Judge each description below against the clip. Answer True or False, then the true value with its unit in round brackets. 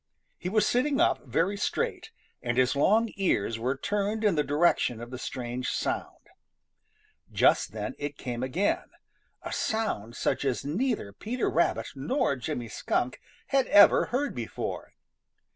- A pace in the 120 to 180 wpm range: True (145 wpm)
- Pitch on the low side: False (150 Hz)